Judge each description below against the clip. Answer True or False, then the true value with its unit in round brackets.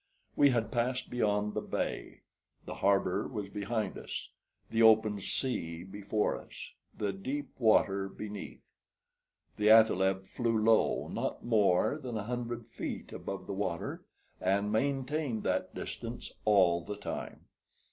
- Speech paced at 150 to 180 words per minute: False (135 wpm)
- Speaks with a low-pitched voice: True (105 Hz)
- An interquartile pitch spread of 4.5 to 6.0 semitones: False (3.2 semitones)